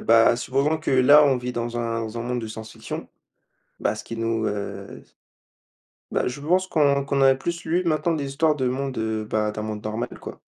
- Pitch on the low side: Yes, low, 125 Hz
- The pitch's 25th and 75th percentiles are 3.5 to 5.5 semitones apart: Yes, average, 4.2 semitones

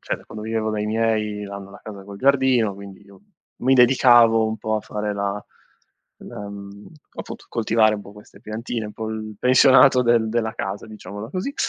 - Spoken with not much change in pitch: Yes, narrow, 2.2 semitones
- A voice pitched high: No, low, 110 Hz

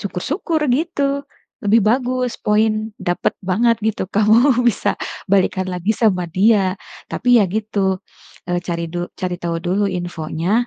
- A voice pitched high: Yes, high, 205 Hz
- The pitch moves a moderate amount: Yes, average, 4.6 semitones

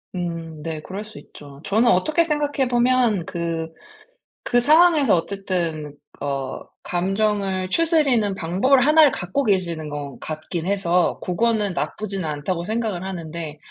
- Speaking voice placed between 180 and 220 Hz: Yes, high, 190 Hz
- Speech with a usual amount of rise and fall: No, wide, 6.0 semitones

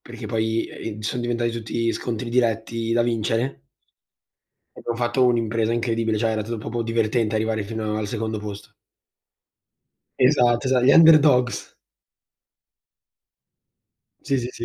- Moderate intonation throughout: No, narrow, 1.5 semitones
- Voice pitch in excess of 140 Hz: No, low, 115 Hz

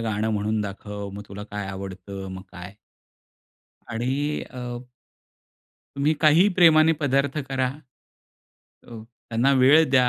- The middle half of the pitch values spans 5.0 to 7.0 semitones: Yes, average, 5.3 semitones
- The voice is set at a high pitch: No, low, 115 Hz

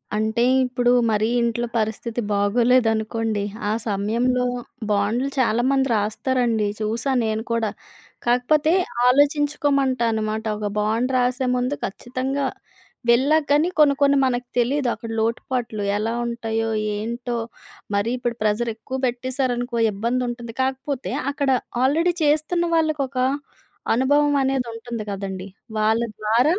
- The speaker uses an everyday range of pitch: Yes, average, 3.2 semitones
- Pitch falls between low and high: No, high, 245 Hz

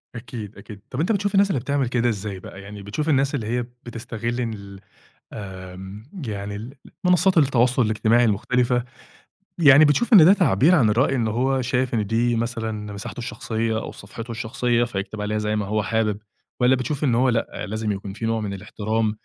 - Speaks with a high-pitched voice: No, low, 115 Hz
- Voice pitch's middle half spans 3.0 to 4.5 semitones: Yes, average, 3.4 semitones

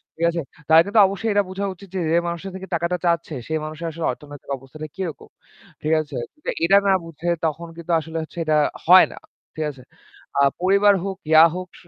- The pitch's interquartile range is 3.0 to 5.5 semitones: Yes, average, 3.3 semitones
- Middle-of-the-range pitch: Yes, medium, 170 Hz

